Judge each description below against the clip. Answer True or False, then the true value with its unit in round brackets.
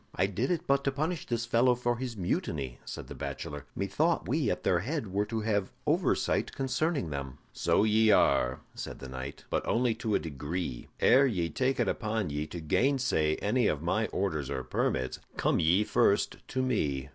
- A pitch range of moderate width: False (8.2 semitones)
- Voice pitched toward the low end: True (105 Hz)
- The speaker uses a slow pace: False (190 wpm)